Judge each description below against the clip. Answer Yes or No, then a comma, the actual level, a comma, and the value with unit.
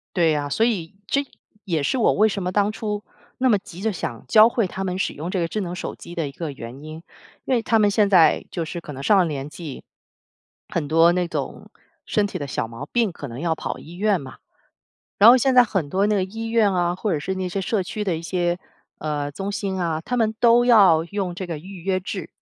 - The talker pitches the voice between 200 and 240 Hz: No, medium, 185 Hz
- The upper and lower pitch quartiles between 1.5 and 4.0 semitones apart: No, average, 4.4 semitones